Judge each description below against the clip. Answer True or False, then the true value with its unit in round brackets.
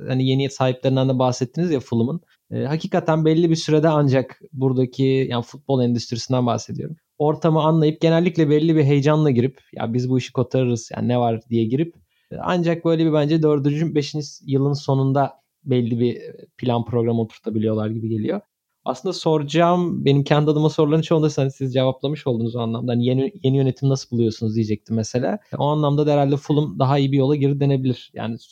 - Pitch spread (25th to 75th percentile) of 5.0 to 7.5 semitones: False (3.9 semitones)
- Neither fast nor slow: False (180 wpm)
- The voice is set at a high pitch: False (135 Hz)